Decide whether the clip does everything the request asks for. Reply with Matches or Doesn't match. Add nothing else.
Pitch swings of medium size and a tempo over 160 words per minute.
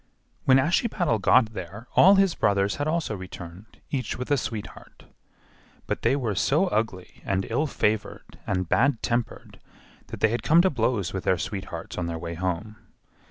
Doesn't match